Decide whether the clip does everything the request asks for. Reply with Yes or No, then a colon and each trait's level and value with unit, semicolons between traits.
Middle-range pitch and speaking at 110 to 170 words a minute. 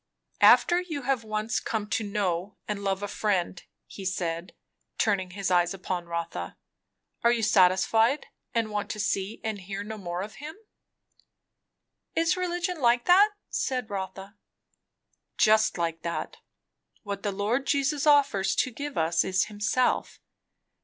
No: high, 210 Hz; average, 145 wpm